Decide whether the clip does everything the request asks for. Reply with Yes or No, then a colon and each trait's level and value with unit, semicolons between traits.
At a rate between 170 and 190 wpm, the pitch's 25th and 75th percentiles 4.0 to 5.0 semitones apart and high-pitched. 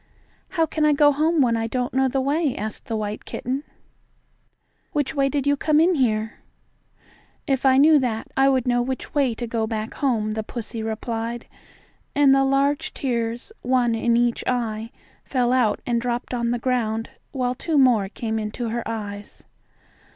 No: average, 180 wpm; average, 3.2 semitones; high, 245 Hz